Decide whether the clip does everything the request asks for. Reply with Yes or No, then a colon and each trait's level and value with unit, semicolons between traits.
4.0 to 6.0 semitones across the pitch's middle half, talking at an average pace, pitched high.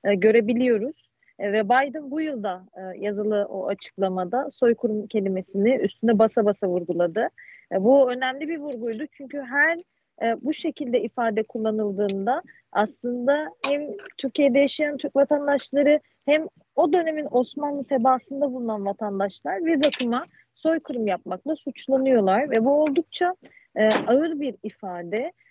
Yes: wide, 5.4 semitones; average, 125 wpm; very high, 255 Hz